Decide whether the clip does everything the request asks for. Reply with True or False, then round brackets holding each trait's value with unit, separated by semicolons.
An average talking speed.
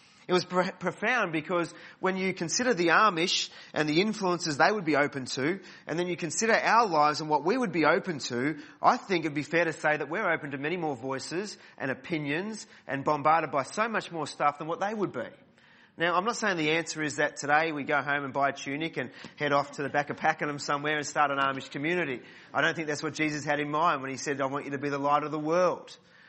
False (250 wpm)